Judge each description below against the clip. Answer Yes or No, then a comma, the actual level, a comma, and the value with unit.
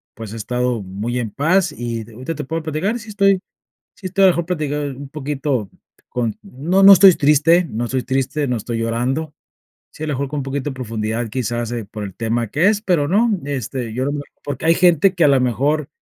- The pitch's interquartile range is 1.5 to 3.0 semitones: No, wide, 5.5 semitones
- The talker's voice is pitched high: No, low, 135 Hz